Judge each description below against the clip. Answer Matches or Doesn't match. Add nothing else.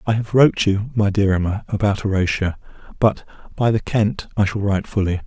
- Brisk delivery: Doesn't match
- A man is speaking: Matches